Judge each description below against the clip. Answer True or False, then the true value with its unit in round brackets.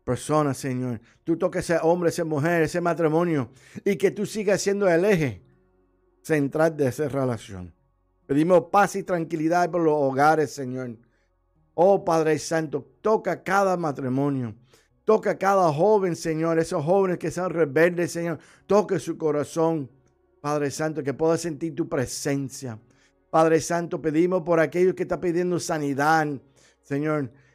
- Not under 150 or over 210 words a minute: False (140 wpm)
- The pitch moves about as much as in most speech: True (4.0 semitones)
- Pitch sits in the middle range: True (160 Hz)